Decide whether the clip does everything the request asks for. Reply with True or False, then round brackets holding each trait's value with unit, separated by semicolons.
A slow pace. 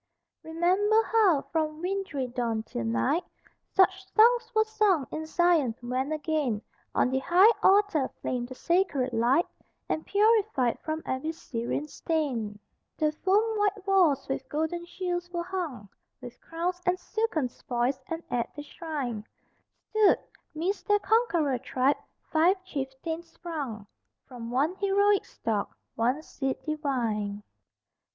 True (130 wpm)